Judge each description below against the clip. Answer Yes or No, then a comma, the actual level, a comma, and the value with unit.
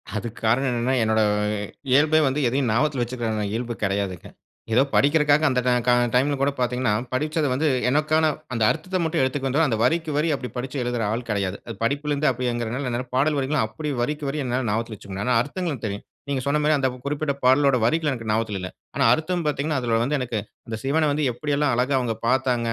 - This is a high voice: No, low, 130 Hz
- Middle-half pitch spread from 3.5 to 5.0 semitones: Yes, average, 3.9 semitones